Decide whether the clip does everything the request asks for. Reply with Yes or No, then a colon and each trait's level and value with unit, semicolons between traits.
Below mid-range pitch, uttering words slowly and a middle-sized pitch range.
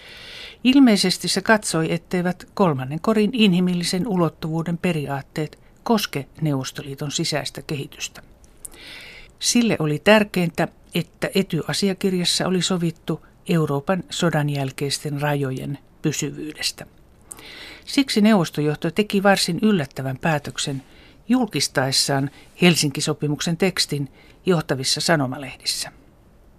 No: medium, 165 Hz; slow, 80 wpm; average, 4.8 semitones